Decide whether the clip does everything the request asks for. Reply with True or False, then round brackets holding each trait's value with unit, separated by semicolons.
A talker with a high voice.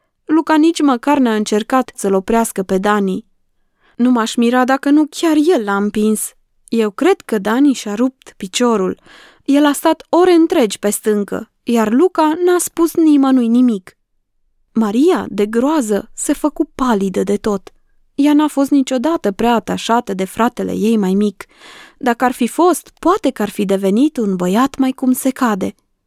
True (250 Hz)